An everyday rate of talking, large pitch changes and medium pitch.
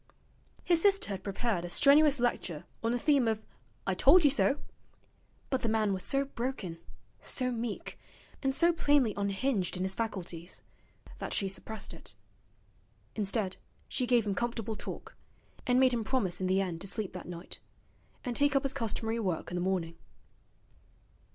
No: average, 170 wpm; wide, 5.7 semitones; high, 225 Hz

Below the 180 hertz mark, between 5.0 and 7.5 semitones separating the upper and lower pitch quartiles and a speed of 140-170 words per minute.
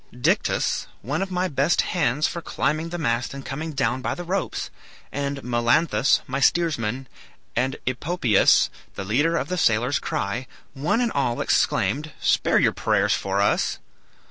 Yes: medium, 140 Hz; wide, 5.5 semitones; average, 155 wpm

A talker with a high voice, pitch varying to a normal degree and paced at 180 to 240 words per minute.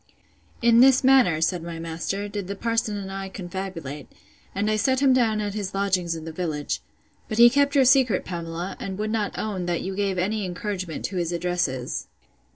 Yes: high, 195 Hz; average, 3.7 semitones; average, 195 wpm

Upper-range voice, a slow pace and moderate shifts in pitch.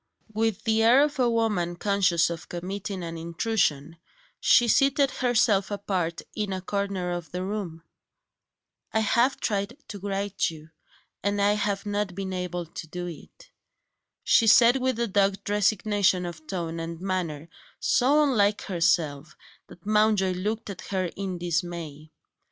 No: high, 195 Hz; average, 155 wpm; average, 3.6 semitones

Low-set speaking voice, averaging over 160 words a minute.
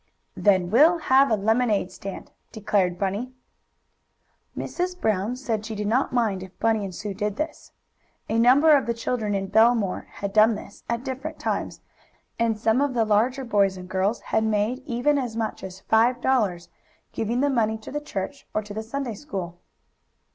No: high, 220 Hz; average, 180 wpm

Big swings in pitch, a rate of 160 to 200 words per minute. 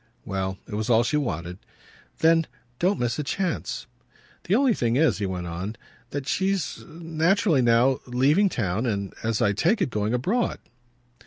Yes: wide, 8.0 semitones; average, 165 wpm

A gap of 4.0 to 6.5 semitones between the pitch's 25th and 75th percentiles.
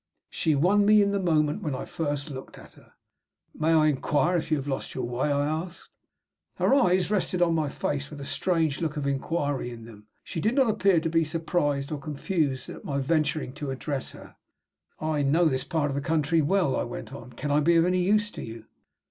No: average, 3.5 semitones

